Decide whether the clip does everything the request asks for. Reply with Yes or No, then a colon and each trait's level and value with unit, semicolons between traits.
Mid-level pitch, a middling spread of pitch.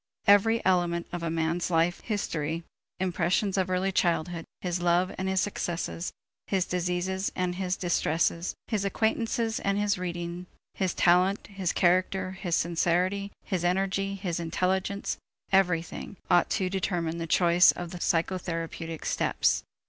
No: medium, 180 Hz; narrow, 2.0 semitones